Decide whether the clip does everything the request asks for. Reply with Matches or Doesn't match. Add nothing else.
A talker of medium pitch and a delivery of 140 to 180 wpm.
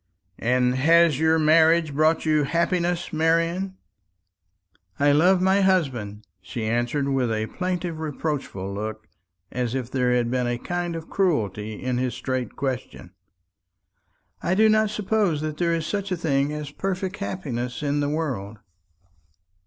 Matches